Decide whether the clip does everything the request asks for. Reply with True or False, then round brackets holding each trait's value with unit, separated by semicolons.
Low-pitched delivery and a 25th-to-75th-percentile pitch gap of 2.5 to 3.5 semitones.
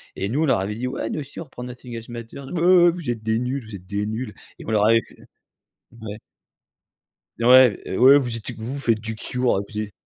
True (115 Hz; 3.1 semitones)